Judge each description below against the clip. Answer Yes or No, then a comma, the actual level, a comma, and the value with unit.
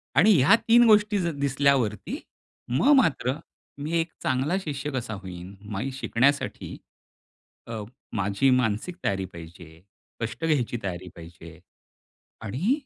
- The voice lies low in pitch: Yes, low, 130 Hz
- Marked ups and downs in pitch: Yes, wide, 7.6 semitones